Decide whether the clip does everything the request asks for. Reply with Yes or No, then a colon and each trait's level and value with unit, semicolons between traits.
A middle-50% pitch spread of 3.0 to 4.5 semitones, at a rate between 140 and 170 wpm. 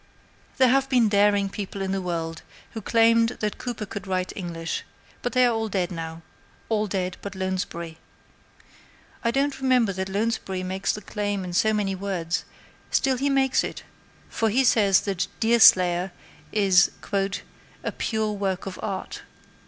Yes: average, 3.6 semitones; average, 160 wpm